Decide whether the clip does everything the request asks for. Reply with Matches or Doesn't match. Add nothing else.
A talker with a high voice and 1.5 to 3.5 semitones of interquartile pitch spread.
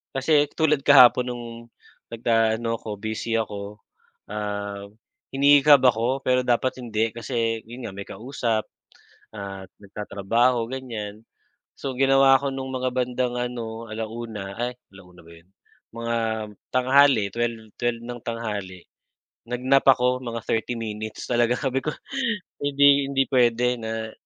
Doesn't match